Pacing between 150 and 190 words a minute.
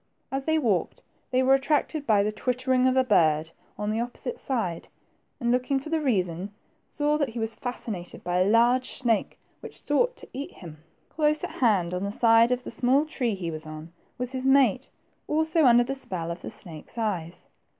No: average, 200 wpm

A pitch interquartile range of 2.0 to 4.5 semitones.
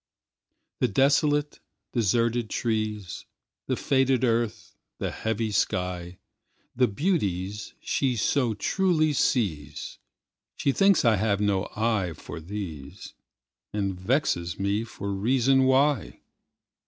No: average, 5.2 semitones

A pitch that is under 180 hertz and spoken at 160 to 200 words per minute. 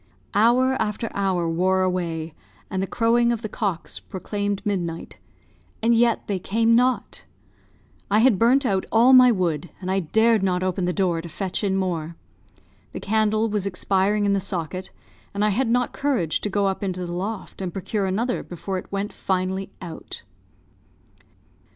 No: high, 195 Hz; average, 170 wpm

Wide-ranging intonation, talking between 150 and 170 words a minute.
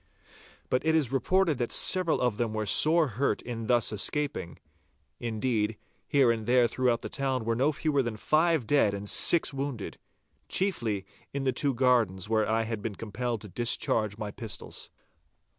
No: average, 4.3 semitones; average, 165 wpm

